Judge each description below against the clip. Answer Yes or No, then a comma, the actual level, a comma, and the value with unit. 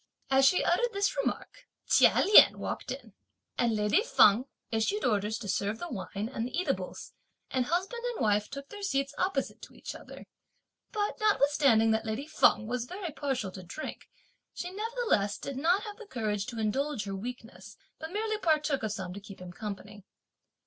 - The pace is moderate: Yes, average, 180 wpm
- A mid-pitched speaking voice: No, very high, 260 Hz